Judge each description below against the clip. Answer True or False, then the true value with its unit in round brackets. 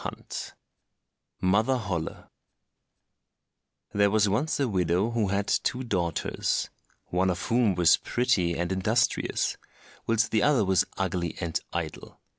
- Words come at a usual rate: False (120 wpm)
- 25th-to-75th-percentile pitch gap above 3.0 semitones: True (4.5 semitones)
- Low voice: True (100 Hz)